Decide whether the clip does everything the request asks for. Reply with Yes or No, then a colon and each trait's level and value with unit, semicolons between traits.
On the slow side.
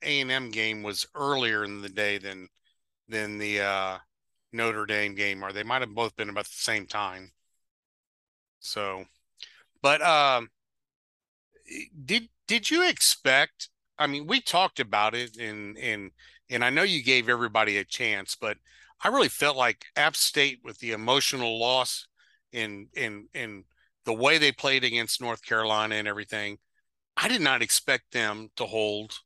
No: average, 165 wpm